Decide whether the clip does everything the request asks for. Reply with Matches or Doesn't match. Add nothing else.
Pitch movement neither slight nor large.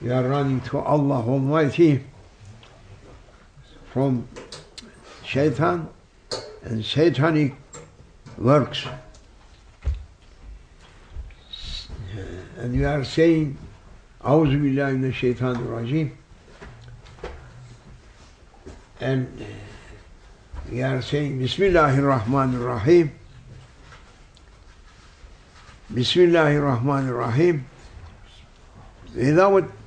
Doesn't match